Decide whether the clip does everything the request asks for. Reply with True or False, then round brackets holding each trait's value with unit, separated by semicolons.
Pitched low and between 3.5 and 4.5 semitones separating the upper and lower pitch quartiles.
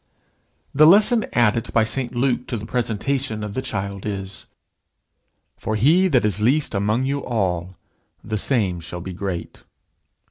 False (110 Hz; 4.9 semitones)